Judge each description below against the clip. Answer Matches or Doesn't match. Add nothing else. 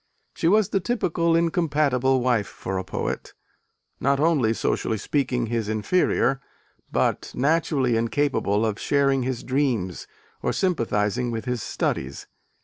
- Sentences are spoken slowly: Matches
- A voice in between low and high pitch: Doesn't match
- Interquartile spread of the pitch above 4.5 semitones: Matches